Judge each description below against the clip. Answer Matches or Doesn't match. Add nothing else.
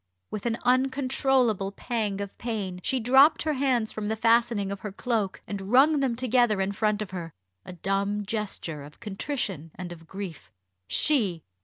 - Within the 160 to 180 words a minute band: Matches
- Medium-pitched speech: Doesn't match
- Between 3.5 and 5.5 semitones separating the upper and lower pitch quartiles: Matches